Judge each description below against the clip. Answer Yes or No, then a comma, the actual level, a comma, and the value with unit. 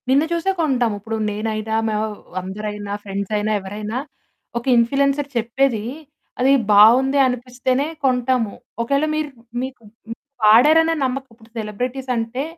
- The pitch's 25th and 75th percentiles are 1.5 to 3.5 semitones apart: No, average, 3.9 semitones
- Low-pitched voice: No, high, 235 Hz